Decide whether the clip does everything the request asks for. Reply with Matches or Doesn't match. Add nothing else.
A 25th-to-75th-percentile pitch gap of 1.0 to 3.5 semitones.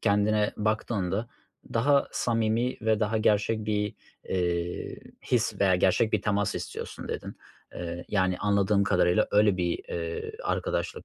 Matches